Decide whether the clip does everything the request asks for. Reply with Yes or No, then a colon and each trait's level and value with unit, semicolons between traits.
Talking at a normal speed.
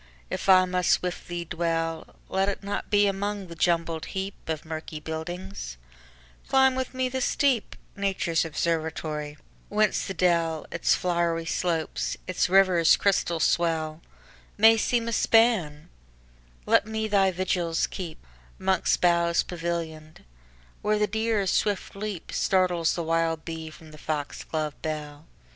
No: slow, 120 wpm